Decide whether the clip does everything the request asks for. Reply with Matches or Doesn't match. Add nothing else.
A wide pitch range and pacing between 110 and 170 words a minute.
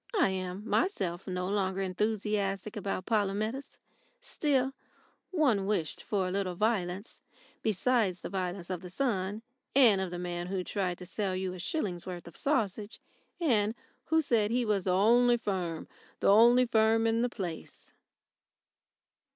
Doesn't match